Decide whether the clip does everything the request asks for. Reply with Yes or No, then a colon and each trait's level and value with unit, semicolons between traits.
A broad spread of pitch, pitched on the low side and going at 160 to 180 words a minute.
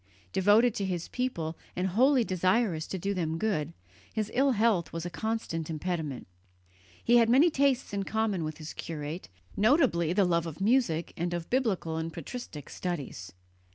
No: wide, 5.7 semitones; medium, 185 Hz; average, 165 wpm